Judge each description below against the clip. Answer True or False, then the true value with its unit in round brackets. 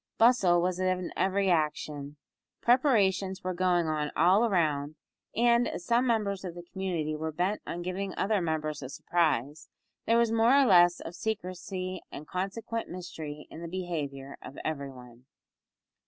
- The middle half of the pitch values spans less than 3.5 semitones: False (4.3 semitones)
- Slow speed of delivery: False (155 wpm)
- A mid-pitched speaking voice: True (180 Hz)